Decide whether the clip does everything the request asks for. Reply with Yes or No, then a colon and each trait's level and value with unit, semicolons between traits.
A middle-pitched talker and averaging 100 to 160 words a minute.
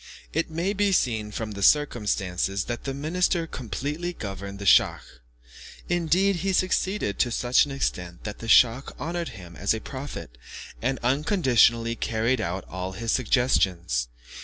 No: low, 120 Hz; average, 150 wpm